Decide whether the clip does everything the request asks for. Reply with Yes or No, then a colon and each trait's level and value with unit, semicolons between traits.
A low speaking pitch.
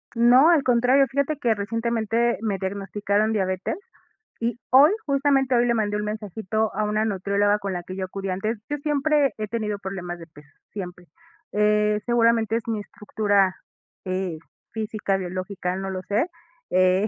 No: high, 210 Hz